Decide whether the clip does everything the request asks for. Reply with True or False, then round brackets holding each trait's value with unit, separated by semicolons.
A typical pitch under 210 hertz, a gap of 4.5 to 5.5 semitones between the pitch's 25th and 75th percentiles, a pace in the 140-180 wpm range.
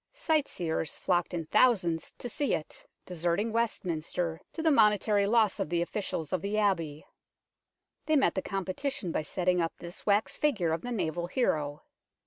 True (185 Hz; 4.8 semitones; 160 wpm)